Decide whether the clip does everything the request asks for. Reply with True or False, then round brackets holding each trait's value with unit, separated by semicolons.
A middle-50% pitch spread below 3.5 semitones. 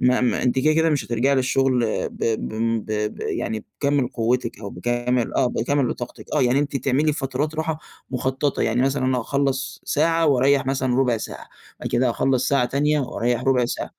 True (2.5 semitones)